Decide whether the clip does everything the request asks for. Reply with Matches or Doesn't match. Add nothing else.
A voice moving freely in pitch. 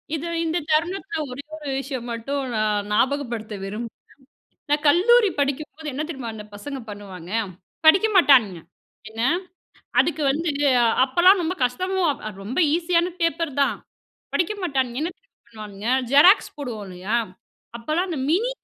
Matches